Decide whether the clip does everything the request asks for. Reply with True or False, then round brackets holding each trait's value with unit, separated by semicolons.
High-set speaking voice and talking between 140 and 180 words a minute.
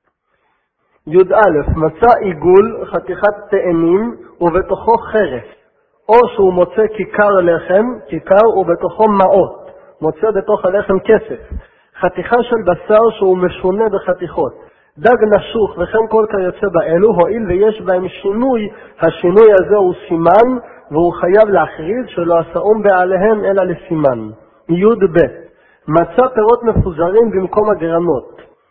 False (195 Hz; 115 wpm)